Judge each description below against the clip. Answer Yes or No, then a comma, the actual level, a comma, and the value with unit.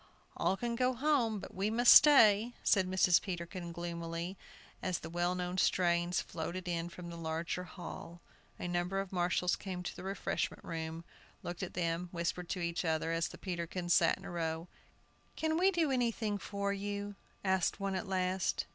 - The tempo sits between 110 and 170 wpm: No, average, 180 wpm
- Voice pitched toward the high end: No, medium, 180 Hz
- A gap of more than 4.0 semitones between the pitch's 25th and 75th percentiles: No, average, 2.8 semitones